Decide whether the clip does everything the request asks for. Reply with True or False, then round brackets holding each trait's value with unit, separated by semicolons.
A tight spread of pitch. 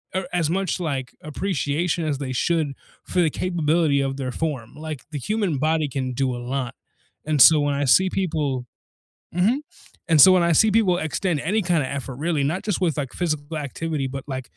False (4.1 semitones)